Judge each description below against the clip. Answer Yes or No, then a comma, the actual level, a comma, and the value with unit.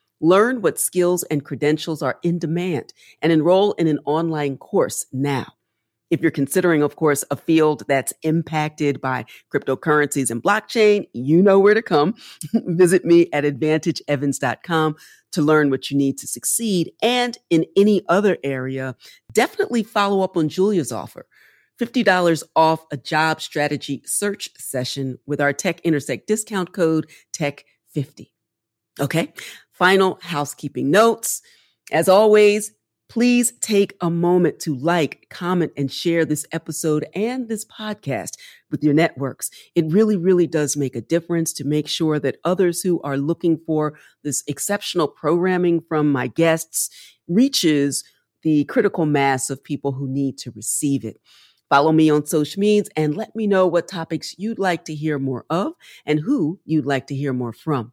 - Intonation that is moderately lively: Yes, average, 4.4 semitones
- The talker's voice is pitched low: No, medium, 160 Hz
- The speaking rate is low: No, average, 155 wpm